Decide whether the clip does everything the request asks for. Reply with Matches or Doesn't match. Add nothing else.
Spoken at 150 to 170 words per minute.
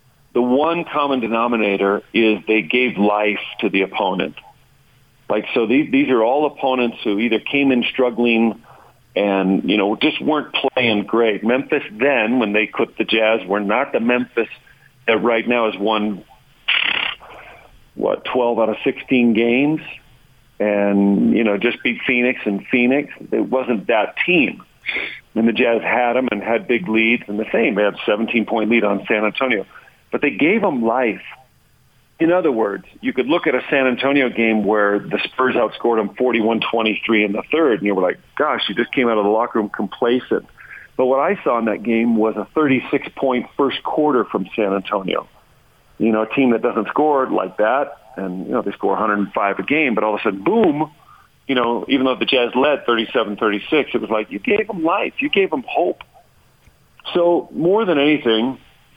Doesn't match